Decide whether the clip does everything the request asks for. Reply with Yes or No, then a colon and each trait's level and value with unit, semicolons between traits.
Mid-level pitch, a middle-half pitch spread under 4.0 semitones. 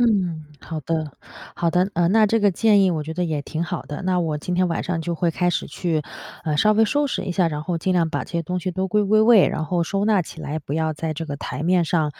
Yes: medium, 175 Hz; average, 3.0 semitones